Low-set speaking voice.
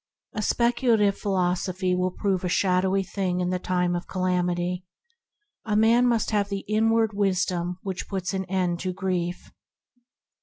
No: medium, 185 Hz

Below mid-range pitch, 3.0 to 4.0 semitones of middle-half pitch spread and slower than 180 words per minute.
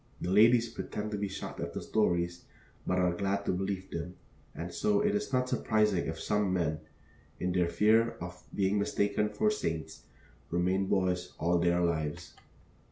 Yes: very low, 95 Hz; average, 3.3 semitones; average, 170 wpm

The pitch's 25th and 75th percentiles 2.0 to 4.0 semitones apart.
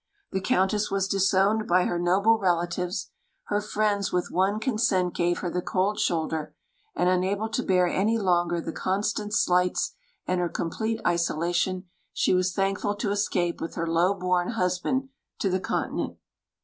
Yes: average, 2.7 semitones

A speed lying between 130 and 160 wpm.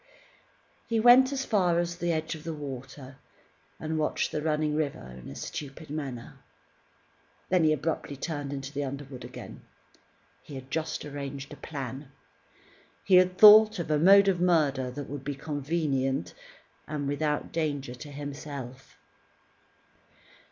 Yes: average, 145 wpm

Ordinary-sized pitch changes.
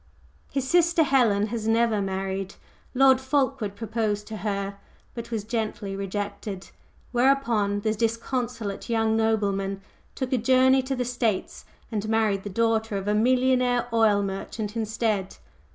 Yes: average, 3.4 semitones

